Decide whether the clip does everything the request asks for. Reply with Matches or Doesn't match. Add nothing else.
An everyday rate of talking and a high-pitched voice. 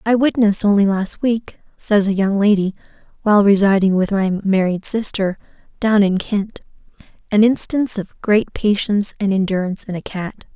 Matches